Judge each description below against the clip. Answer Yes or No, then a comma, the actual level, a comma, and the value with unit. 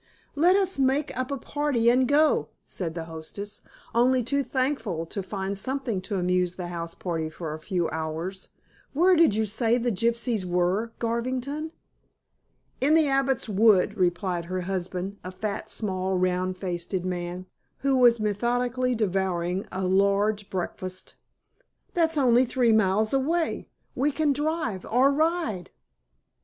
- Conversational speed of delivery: Yes, average, 145 wpm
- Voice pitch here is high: Yes, high, 215 Hz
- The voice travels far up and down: Yes, wide, 6.0 semitones